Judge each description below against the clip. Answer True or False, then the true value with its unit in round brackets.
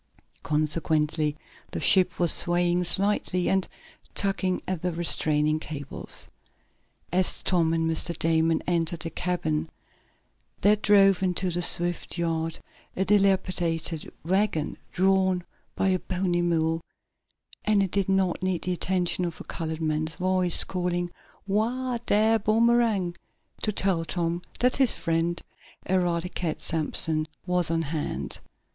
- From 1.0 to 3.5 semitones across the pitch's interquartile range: True (2.6 semitones)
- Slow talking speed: True (125 wpm)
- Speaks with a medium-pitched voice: True (175 Hz)